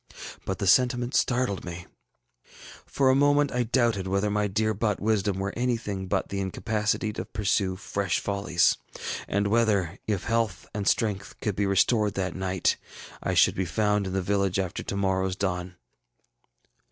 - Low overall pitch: Yes, low, 100 Hz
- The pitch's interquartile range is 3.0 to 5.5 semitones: No, narrow, 2.5 semitones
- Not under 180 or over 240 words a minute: No, average, 165 wpm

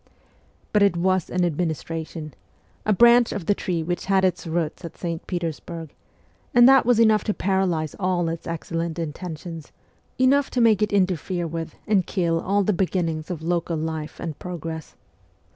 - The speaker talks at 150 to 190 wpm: Yes, average, 165 wpm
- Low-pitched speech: No, medium, 175 Hz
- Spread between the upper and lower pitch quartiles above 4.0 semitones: No, average, 3.0 semitones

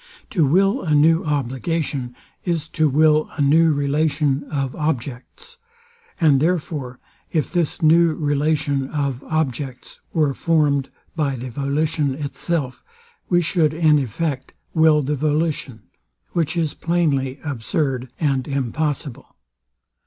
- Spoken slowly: Yes, slow, 120 wpm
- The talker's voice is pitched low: No, medium, 150 Hz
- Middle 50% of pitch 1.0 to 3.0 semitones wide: Yes, average, 2.7 semitones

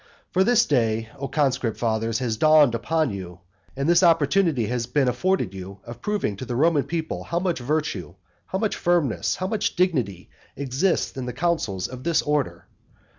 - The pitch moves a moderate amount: No, wide, 6.7 semitones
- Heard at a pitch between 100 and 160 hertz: Yes, low, 135 Hz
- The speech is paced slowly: No, average, 180 wpm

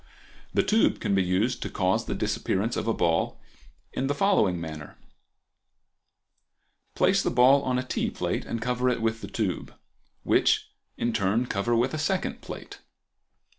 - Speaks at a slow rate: No, average, 160 wpm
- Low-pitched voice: Yes, low, 115 Hz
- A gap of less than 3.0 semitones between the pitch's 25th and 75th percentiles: No, average, 4.7 semitones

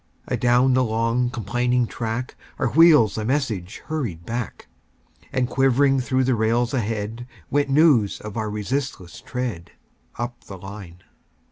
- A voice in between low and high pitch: No, low, 120 Hz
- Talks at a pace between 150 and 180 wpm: No, slow, 135 wpm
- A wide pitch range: No, average, 3.5 semitones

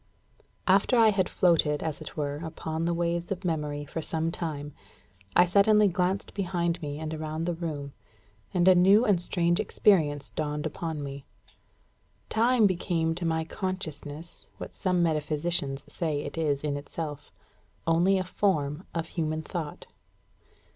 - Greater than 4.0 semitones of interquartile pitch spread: No, average, 3.3 semitones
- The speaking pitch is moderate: Yes, medium, 165 Hz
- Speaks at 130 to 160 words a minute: Yes, average, 150 wpm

